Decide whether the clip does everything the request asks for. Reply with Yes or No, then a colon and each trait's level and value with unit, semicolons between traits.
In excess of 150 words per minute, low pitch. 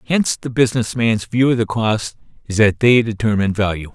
Yes: average, 200 wpm; low, 115 Hz